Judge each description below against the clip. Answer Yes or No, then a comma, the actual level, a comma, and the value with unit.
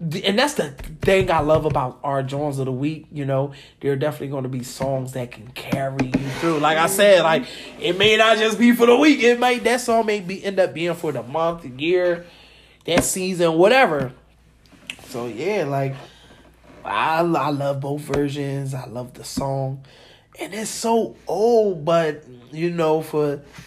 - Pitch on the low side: No, medium, 155 Hz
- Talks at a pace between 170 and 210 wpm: Yes, average, 190 wpm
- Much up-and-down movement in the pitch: Yes, wide, 5.7 semitones